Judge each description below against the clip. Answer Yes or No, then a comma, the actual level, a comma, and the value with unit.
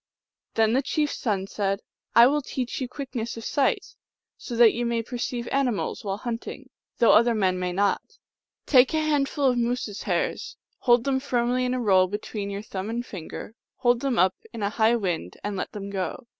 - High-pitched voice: Yes, high, 235 Hz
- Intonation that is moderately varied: Yes, average, 3.9 semitones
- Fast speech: Yes, fast, 215 wpm